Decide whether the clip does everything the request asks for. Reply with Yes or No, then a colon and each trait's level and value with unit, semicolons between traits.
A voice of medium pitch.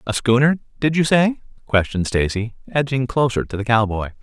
No: low, 125 Hz